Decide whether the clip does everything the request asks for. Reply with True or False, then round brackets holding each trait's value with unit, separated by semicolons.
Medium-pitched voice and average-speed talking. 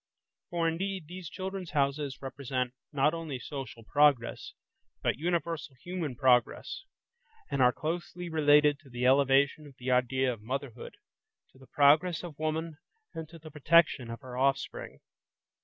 True (145 Hz; 145 wpm)